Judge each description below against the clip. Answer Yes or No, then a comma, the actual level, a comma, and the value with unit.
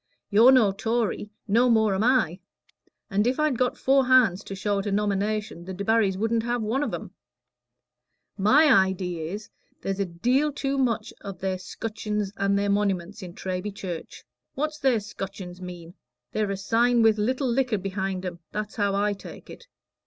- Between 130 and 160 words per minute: No, average, 175 wpm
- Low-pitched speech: No, high, 210 Hz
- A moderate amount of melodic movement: Yes, average, 3.6 semitones